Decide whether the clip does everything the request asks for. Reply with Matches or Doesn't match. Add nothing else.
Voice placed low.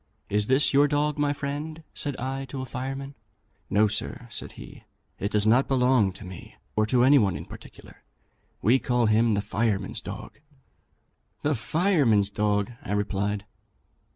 Matches